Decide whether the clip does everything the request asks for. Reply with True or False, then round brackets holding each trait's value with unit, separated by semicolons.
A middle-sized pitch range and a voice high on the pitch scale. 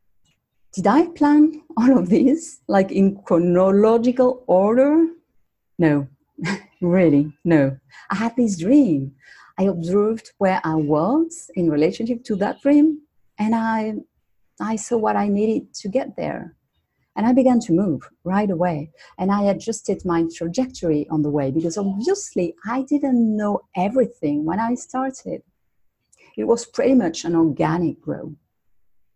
False (6.9 semitones; 205 Hz)